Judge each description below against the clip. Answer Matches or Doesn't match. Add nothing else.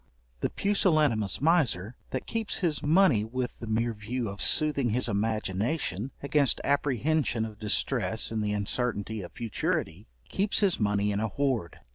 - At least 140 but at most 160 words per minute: Matches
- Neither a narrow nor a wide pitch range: Doesn't match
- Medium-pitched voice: Doesn't match